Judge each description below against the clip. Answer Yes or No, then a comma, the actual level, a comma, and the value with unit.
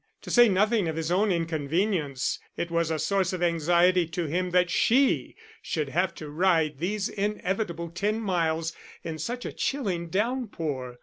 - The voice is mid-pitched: Yes, medium, 175 Hz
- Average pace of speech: Yes, average, 165 wpm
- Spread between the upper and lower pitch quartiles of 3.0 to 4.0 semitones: Yes, average, 3.6 semitones